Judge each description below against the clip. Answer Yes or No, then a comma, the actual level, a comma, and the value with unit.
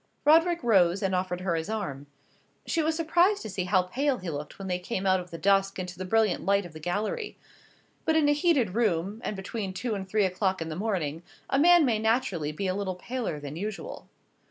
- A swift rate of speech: Yes, fast, 225 wpm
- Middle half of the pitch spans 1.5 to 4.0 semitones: No, average, 4.8 semitones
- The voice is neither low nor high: No, high, 195 Hz